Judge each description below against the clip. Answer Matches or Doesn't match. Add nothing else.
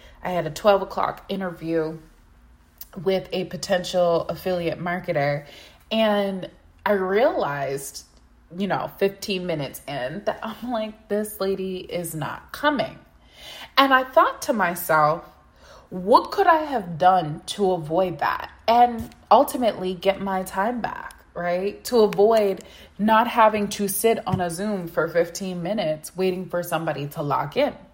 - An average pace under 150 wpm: Matches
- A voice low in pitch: Doesn't match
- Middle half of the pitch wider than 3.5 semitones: Matches